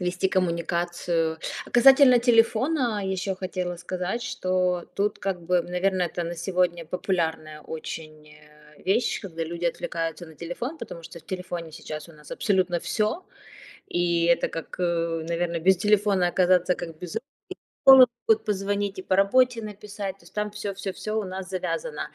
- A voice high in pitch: No, medium, 180 Hz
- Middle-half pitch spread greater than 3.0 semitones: Yes, average, 3.4 semitones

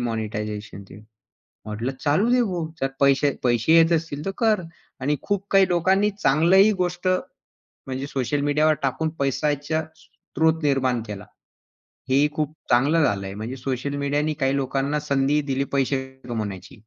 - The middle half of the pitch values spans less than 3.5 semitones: No, average, 3.8 semitones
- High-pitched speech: No, medium, 140 Hz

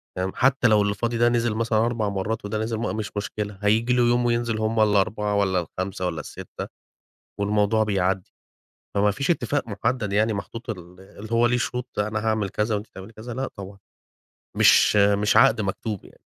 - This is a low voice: Yes, low, 110 Hz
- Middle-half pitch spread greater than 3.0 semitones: No, narrow, 2.4 semitones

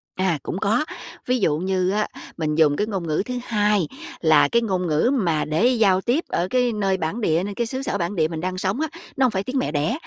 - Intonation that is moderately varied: No, wide, 6.1 semitones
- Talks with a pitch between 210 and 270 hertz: No, high, 190 Hz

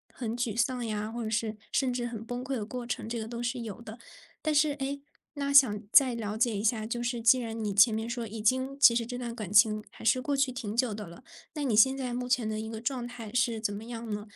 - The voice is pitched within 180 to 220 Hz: No, high, 235 Hz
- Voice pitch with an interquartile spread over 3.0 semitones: No, narrow, 2.5 semitones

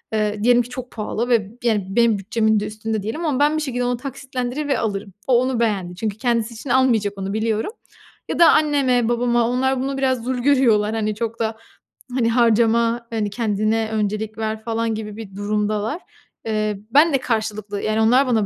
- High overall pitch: Yes, high, 225 Hz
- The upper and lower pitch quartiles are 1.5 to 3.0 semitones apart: Yes, narrow, 2.6 semitones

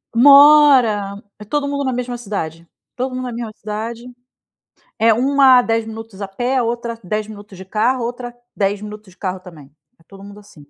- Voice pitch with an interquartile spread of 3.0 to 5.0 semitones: Yes, average, 3.5 semitones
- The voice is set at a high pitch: Yes, high, 225 Hz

